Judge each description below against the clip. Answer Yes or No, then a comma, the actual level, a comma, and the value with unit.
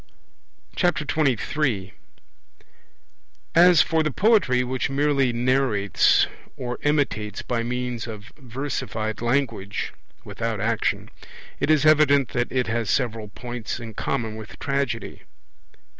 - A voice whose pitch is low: Yes, low, 125 Hz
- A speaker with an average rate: No, slow, 110 wpm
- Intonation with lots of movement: No, average, 3.9 semitones